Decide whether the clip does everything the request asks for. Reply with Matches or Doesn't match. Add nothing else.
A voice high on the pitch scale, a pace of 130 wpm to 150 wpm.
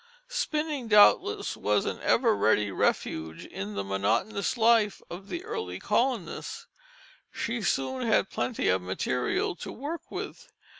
Matches